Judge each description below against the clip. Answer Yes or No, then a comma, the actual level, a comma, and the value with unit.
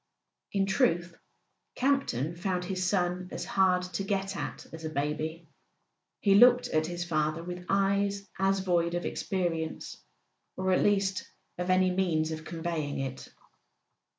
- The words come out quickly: No, average, 145 wpm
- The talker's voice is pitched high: No, medium, 180 Hz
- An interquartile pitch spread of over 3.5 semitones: No, average, 2.9 semitones